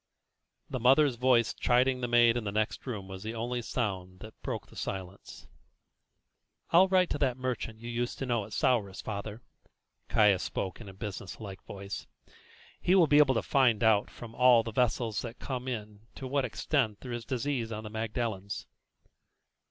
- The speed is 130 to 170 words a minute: No, average, 185 wpm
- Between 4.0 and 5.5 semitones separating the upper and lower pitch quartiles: No, average, 3.3 semitones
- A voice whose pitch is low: Yes, low, 115 Hz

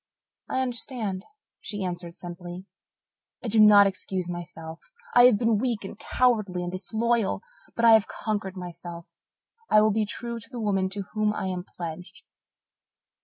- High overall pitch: Yes, high, 200 Hz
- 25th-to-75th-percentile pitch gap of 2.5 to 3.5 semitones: No, average, 3.9 semitones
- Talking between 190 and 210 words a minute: No, average, 160 wpm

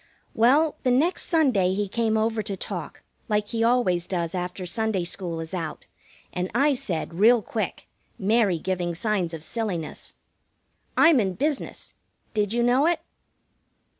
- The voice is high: Yes, high, 210 Hz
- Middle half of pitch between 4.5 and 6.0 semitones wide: Yes, average, 5.0 semitones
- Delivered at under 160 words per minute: Yes, average, 150 wpm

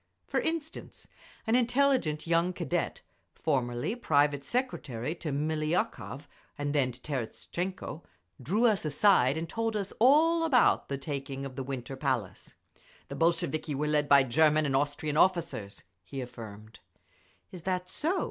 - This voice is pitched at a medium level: Yes, medium, 155 Hz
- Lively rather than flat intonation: Yes, wide, 5.7 semitones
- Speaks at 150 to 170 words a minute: No, average, 140 wpm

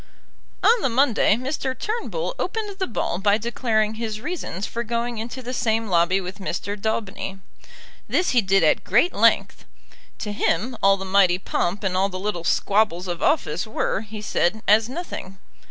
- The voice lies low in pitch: No, high, 215 Hz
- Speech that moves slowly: No, average, 170 wpm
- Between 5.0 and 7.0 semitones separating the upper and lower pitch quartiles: No, average, 4.0 semitones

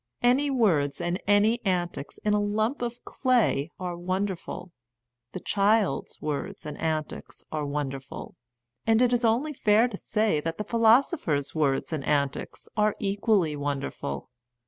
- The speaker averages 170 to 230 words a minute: No, average, 145 wpm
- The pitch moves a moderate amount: No, wide, 6.8 semitones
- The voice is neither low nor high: No, high, 195 Hz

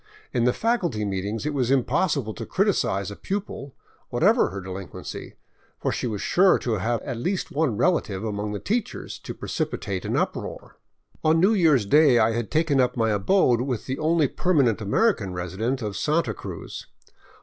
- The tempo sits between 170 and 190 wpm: Yes, average, 175 wpm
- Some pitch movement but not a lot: No, wide, 7.2 semitones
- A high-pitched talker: No, low, 125 Hz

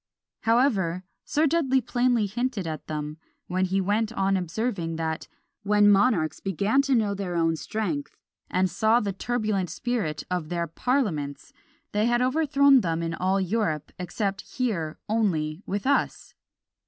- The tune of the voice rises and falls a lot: Yes, wide, 6.0 semitones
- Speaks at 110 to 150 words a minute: Yes, average, 145 wpm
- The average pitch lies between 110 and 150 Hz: No, high, 200 Hz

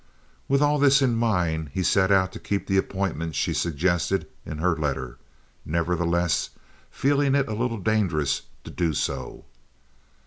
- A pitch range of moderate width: No, wide, 5.7 semitones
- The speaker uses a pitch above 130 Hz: No, very low, 95 Hz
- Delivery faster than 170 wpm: No, average, 150 wpm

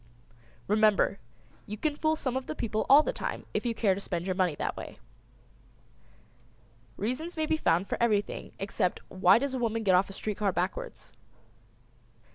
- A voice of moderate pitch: No, high, 215 Hz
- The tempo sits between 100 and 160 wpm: No, average, 185 wpm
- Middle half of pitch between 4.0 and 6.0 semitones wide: Yes, average, 5.3 semitones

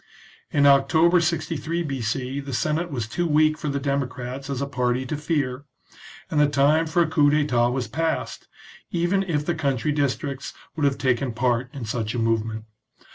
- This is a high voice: No, medium, 140 Hz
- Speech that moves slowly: No, average, 180 wpm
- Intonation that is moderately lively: Yes, average, 3.7 semitones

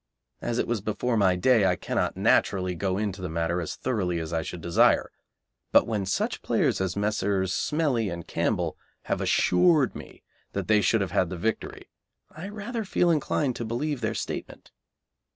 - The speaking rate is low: No, average, 180 wpm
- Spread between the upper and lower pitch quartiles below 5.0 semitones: No, wide, 5.4 semitones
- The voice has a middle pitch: No, low, 105 Hz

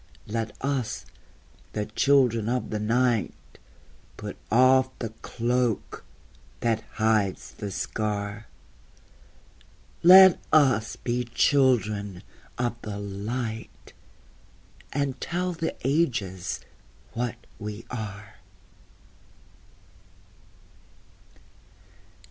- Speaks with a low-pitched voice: Yes, low, 115 Hz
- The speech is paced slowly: Yes, slow, 80 wpm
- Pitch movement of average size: Yes, average, 3.4 semitones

